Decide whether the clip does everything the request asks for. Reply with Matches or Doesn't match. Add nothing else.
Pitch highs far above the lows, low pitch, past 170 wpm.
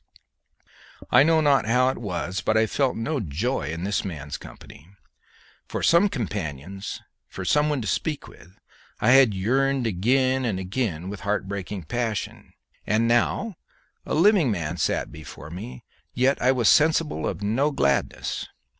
Doesn't match